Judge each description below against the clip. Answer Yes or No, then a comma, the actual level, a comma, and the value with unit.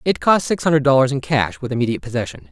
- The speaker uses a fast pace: Yes, fast, 240 wpm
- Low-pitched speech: Yes, low, 130 Hz